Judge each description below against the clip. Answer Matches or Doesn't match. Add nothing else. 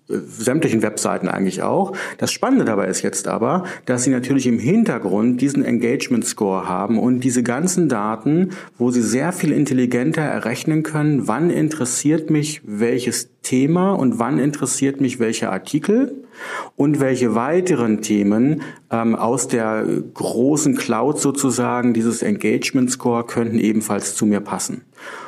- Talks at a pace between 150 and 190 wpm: Doesn't match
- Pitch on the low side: Matches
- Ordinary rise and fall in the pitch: Matches